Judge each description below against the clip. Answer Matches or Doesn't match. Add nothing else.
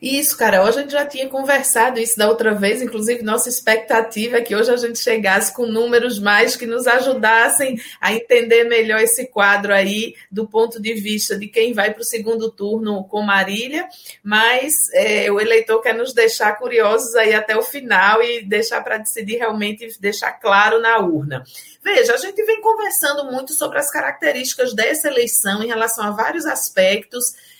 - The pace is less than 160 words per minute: Doesn't match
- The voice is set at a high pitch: Matches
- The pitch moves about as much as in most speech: Matches